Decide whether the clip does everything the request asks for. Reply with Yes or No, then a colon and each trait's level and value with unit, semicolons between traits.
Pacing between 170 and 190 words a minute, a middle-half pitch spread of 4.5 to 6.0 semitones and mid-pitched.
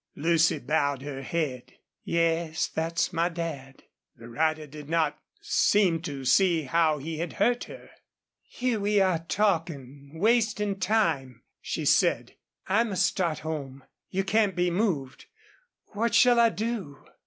No: average, 140 wpm; average, 5.0 semitones; medium, 165 Hz